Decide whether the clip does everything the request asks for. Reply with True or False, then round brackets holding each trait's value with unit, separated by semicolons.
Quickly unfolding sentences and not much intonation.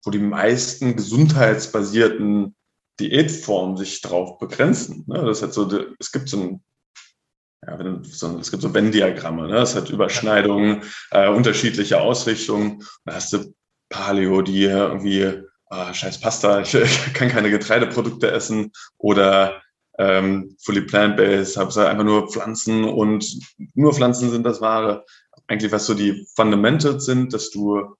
False (145 wpm; 2.3 semitones)